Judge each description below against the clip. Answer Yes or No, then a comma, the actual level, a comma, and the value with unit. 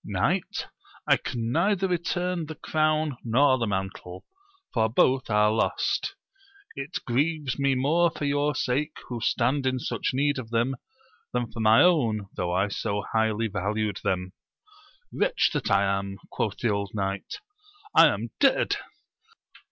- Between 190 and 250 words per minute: No, average, 150 wpm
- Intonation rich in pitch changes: Yes, wide, 5.7 semitones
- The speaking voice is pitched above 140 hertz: No, low, 120 Hz